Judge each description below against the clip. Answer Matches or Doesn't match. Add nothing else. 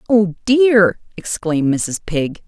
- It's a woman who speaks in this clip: Matches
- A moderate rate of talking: Doesn't match